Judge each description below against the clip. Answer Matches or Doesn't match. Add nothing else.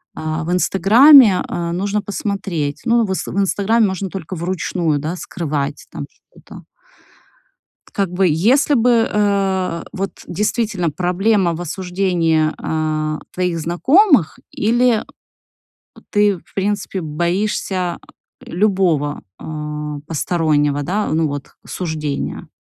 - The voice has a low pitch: Doesn't match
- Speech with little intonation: Doesn't match